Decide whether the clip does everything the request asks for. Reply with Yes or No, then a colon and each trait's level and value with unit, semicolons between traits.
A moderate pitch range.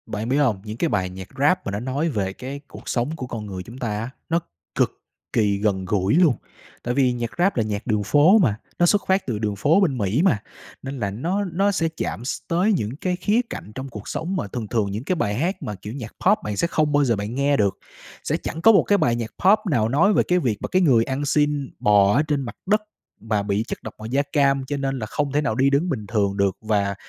No: wide, 6.7 semitones